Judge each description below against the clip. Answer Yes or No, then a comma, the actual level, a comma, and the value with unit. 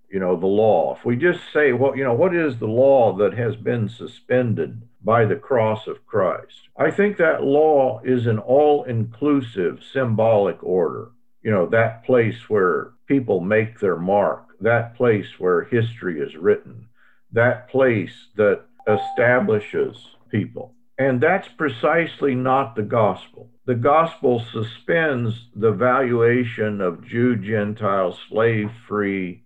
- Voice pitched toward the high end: No, low, 120 Hz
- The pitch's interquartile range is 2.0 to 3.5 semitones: No, average, 4.1 semitones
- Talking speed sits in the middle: Yes, average, 145 wpm